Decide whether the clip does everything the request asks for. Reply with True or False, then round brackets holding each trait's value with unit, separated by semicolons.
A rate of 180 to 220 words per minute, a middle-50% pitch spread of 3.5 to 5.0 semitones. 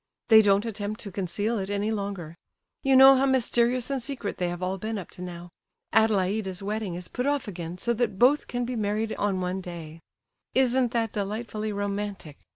True (190 wpm; 3.9 semitones)